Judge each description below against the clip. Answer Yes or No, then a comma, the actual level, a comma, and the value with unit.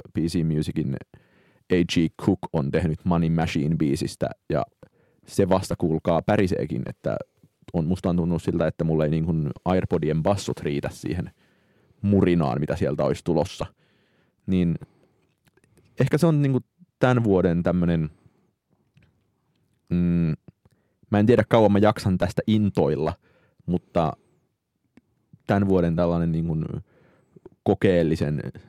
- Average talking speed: Yes, average, 125 wpm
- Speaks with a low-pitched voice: Yes, very low, 90 Hz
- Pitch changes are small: No, average, 3.7 semitones